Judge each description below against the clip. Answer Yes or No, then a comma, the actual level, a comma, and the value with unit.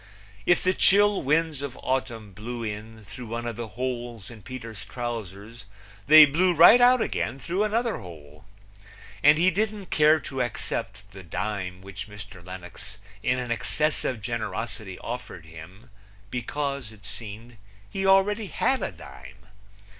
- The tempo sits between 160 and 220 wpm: No, average, 150 wpm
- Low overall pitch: Yes, low, 120 Hz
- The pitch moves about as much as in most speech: No, wide, 6.9 semitones